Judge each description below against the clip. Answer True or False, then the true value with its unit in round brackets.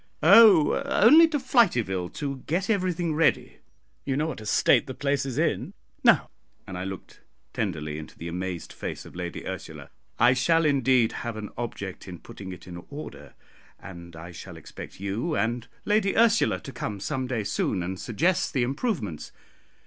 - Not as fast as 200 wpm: True (170 wpm)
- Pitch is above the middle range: False (120 Hz)